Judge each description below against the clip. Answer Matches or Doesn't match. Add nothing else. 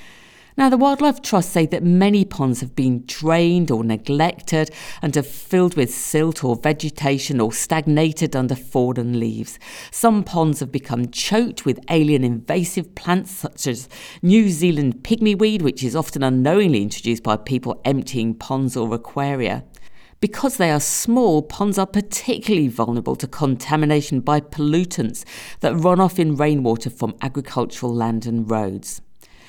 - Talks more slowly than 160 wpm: Matches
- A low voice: Doesn't match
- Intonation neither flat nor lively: Doesn't match